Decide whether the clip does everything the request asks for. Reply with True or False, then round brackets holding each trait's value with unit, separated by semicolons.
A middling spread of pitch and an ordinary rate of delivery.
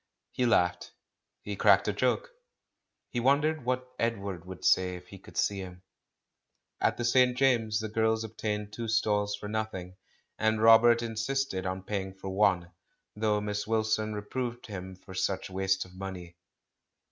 True (3.2 semitones; 160 wpm)